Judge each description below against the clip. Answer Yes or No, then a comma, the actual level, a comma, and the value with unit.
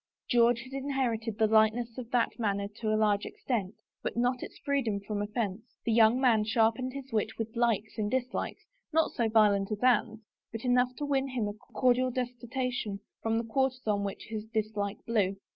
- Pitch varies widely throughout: No, average, 2.7 semitones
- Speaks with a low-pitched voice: No, high, 230 Hz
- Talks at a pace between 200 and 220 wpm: No, average, 190 wpm